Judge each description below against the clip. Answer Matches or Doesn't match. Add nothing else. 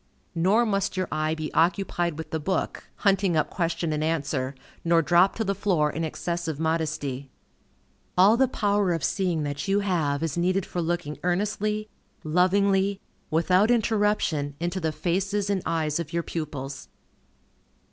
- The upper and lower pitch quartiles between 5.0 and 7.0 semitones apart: Doesn't match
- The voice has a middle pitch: Matches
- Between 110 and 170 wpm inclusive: Matches